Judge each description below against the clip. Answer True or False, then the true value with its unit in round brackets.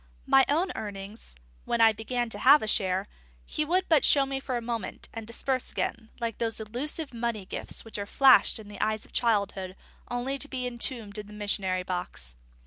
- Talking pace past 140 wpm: True (200 wpm)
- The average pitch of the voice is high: True (230 Hz)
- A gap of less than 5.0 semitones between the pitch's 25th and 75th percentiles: True (4.0 semitones)